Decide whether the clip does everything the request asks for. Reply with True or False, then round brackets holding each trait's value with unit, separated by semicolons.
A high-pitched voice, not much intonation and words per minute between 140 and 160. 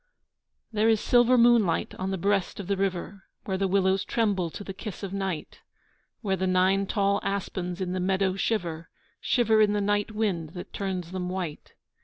False (195 Hz; 2.0 semitones; 185 wpm)